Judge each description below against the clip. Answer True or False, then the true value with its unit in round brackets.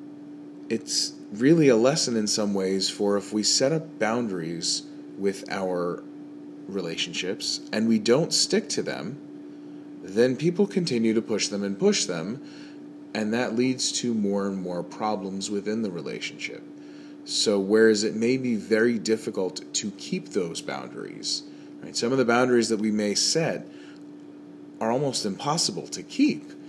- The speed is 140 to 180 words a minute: True (150 wpm)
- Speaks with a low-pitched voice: True (120 Hz)